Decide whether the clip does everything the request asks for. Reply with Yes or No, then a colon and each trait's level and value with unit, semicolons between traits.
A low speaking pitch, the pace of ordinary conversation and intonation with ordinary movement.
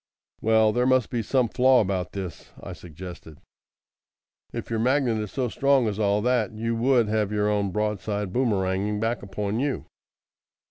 Yes: low, 110 Hz; average, 160 wpm; average, 3.3 semitones